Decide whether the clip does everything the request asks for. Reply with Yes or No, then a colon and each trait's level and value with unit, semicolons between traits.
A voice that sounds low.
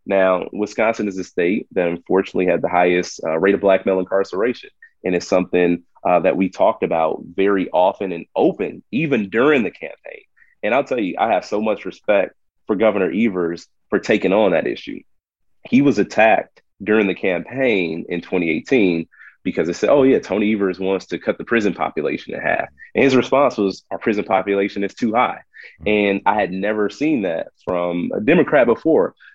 Yes: very low, 95 Hz